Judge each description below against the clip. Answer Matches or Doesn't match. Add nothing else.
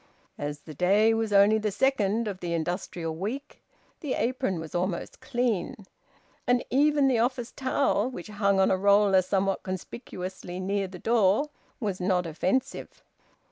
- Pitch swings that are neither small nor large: Matches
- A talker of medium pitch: Doesn't match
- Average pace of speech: Matches